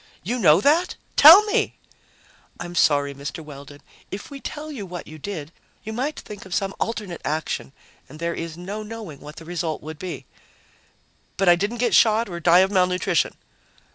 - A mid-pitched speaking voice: Yes, medium, 180 Hz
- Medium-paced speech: Yes, average, 180 wpm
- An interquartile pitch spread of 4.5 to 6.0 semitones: Yes, wide, 5.6 semitones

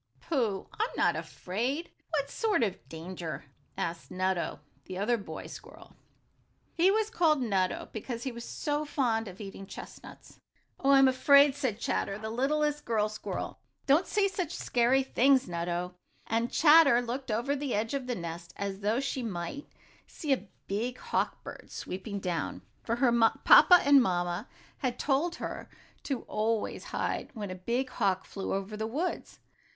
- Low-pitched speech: No, high, 235 Hz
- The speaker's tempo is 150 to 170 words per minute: Yes, average, 160 wpm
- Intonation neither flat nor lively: No, wide, 6.2 semitones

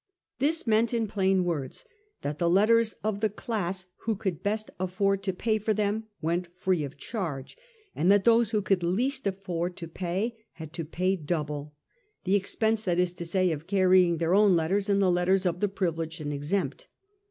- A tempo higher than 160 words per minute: Yes, average, 195 wpm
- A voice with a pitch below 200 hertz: Yes, high, 190 Hz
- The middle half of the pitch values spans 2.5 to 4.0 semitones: Yes, average, 3.6 semitones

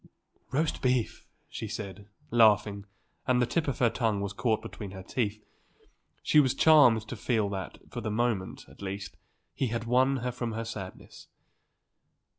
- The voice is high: No, low, 115 Hz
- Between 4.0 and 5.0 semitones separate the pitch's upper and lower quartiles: No, average, 3.5 semitones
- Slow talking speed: No, average, 165 wpm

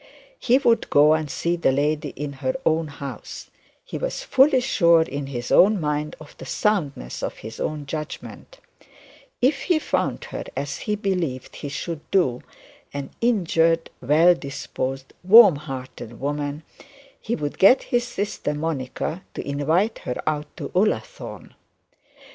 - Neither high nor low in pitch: Yes, medium, 155 Hz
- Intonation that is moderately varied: No, wide, 6.1 semitones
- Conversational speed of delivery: Yes, average, 150 wpm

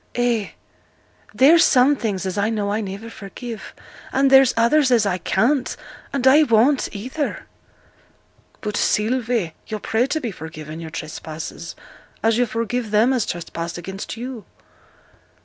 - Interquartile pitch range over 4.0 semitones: Yes, average, 4.4 semitones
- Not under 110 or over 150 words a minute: Yes, average, 145 wpm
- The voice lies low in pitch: No, high, 225 Hz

